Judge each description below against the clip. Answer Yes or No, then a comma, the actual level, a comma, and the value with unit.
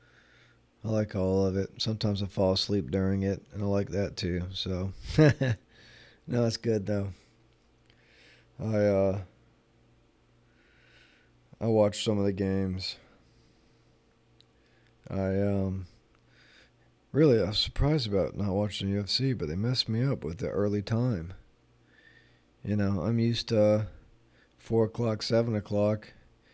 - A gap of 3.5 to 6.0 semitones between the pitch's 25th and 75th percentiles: No, average, 2.7 semitones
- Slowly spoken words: Yes, slow, 130 wpm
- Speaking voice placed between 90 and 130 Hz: Yes, low, 110 Hz